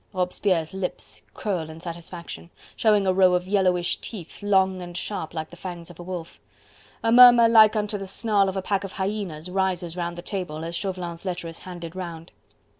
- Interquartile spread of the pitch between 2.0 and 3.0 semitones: Yes, narrow, 2.4 semitones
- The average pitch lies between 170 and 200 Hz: Yes, medium, 185 Hz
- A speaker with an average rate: Yes, average, 190 wpm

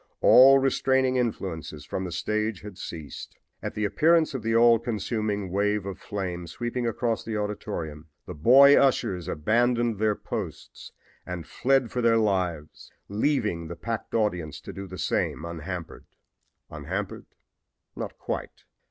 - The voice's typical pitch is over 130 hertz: No, low, 105 Hz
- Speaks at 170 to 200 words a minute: No, average, 145 wpm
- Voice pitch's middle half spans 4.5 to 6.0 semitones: Yes, average, 5.0 semitones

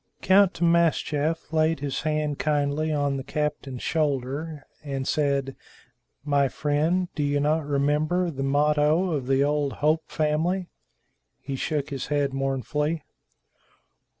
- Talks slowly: Yes, slow, 125 wpm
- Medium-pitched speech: Yes, medium, 150 Hz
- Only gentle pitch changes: Yes, narrow, 2.0 semitones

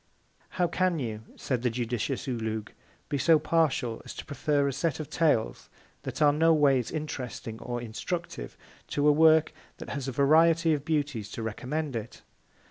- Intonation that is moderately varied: Yes, average, 4.7 semitones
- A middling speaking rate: Yes, average, 170 wpm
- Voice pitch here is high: No, medium, 140 Hz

